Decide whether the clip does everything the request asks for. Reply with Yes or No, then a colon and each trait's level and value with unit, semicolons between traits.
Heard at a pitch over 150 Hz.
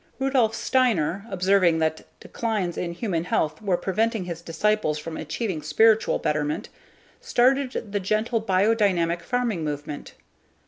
Yes: high, 190 Hz